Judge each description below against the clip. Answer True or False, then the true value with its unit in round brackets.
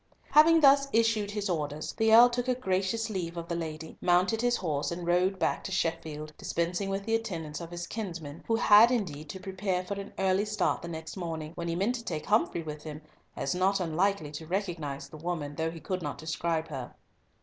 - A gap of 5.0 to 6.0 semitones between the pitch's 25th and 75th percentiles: False (4.3 semitones)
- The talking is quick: True (215 wpm)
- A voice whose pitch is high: False (180 Hz)